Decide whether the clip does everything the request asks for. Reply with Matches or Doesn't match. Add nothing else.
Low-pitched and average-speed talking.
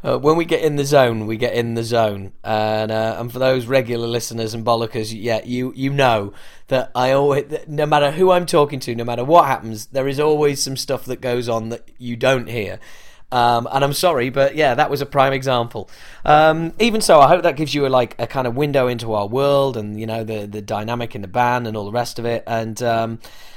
Doesn't match